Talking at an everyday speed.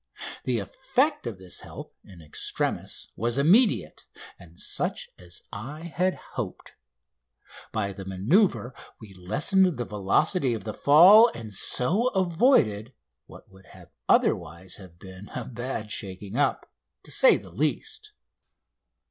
No: slow, 130 wpm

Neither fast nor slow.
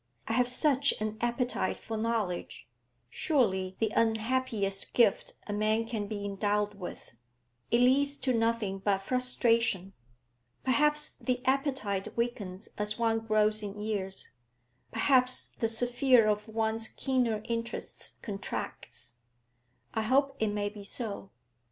No: slow, 125 wpm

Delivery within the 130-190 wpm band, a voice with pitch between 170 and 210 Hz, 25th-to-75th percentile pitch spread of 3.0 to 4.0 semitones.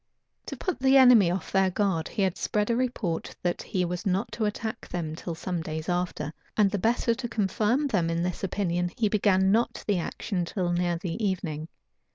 No: fast, 205 wpm; high, 190 Hz; average, 3.7 semitones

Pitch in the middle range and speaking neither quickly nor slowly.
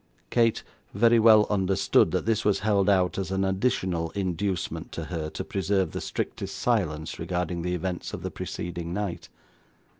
No: very low, 95 Hz; average, 160 wpm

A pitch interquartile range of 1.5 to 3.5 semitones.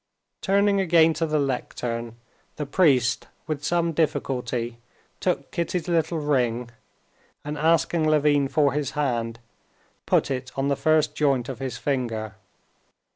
No: average, 4.2 semitones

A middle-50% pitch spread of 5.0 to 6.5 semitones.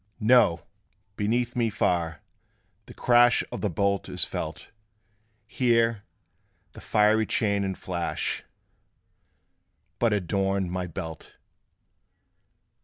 No: average, 4.1 semitones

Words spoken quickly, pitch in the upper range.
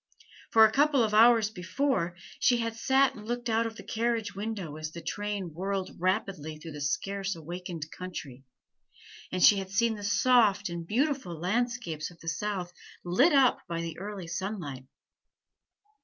No: average, 165 wpm; high, 200 Hz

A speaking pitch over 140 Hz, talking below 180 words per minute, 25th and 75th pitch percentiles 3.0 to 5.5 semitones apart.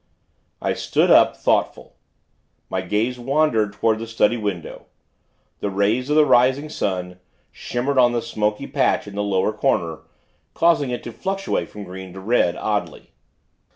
No: low, 110 Hz; average, 155 wpm; average, 4.0 semitones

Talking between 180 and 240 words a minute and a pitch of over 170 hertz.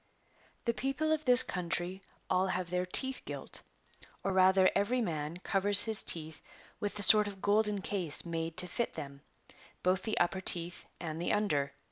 No: average, 170 wpm; high, 190 Hz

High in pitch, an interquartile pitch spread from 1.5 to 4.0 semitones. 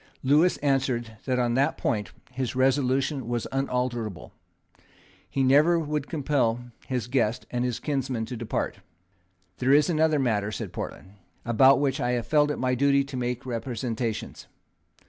No: low, 130 Hz; average, 2.7 semitones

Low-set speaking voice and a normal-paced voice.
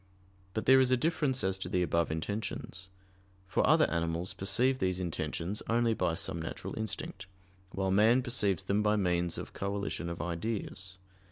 Yes: very low, 95 Hz; average, 165 wpm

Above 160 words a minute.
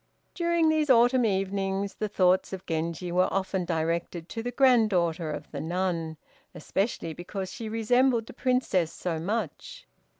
No: average, 145 wpm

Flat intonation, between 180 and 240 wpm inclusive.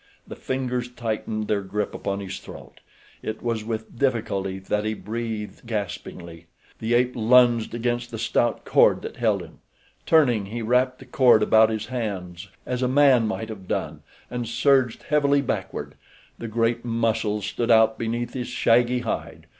No: narrow, 2.3 semitones; average, 160 wpm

